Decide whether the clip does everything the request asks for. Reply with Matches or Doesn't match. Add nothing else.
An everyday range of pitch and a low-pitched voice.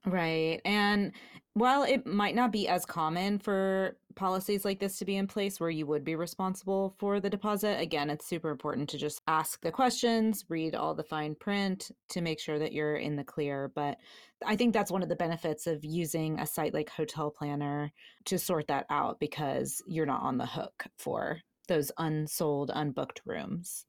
Doesn't match